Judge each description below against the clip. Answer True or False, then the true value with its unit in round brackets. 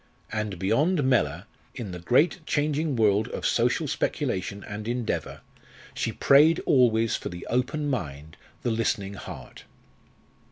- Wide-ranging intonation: True (5.9 semitones)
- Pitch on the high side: False (115 Hz)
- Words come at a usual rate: False (130 wpm)